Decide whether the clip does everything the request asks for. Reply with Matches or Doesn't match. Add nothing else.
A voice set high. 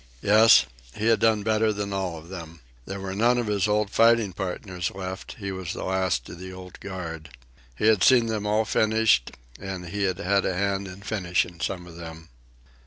Doesn't match